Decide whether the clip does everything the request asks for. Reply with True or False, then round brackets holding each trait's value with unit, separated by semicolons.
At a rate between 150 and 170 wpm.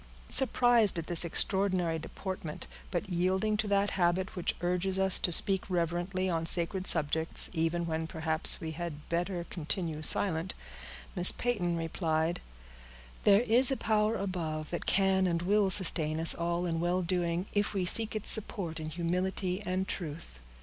True (160 wpm)